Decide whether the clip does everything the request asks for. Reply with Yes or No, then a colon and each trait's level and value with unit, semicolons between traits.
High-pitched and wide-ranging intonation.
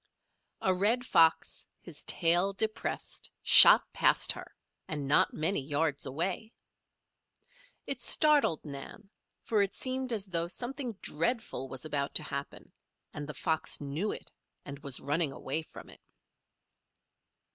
No: medium, 165 Hz; wide, 6.7 semitones